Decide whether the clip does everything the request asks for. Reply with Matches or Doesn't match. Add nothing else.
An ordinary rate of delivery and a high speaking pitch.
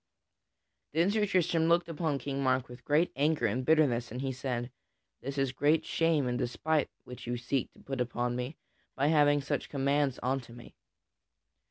Doesn't match